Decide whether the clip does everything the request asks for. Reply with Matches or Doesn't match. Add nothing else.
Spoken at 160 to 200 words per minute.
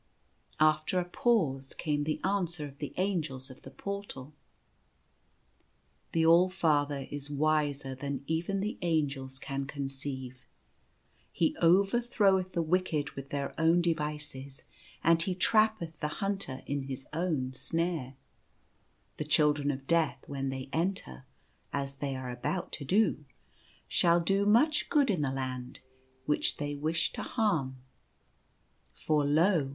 Doesn't match